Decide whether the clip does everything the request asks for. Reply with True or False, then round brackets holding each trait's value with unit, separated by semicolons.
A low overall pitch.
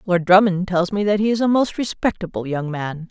False (190 Hz)